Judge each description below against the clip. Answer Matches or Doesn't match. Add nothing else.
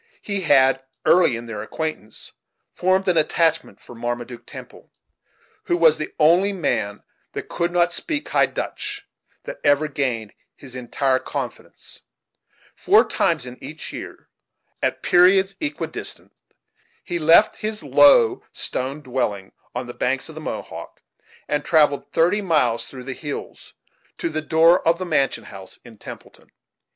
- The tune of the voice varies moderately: Doesn't match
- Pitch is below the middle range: Doesn't match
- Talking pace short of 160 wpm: Matches